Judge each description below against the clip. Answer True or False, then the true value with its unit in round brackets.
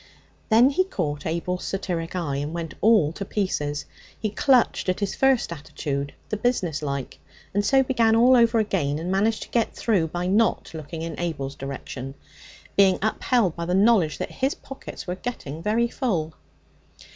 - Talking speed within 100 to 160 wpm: False (170 wpm)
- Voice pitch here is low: False (185 Hz)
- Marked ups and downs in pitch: True (6.4 semitones)